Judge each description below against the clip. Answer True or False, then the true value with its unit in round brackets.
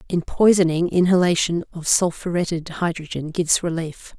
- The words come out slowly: True (115 wpm)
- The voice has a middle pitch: True (170 Hz)